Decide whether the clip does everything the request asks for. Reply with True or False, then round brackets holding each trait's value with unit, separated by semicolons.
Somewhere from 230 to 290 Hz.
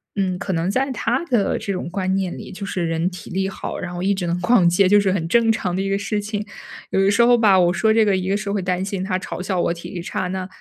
False (190 Hz)